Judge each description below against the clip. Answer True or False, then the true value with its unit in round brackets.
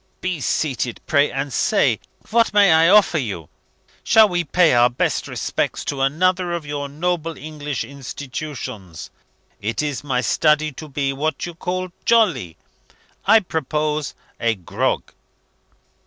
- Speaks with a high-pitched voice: False (150 Hz)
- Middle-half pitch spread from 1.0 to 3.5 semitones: False (4.5 semitones)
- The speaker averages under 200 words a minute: True (140 wpm)